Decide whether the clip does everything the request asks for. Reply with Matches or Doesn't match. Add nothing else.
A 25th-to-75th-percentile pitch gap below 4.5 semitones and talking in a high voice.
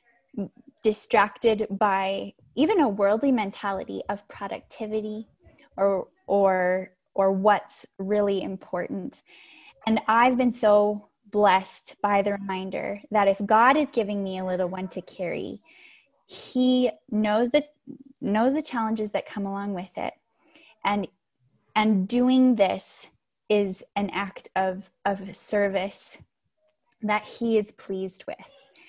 Matches